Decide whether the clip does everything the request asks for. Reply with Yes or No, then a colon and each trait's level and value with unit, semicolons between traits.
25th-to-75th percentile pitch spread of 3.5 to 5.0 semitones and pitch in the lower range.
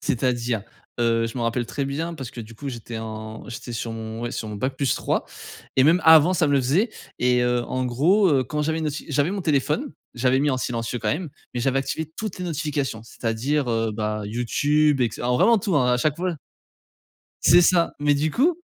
Yes: average, 4.7 semitones; low, 130 Hz